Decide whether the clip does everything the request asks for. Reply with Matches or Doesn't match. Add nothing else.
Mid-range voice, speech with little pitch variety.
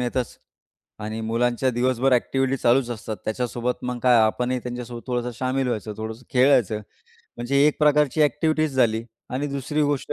Doesn't match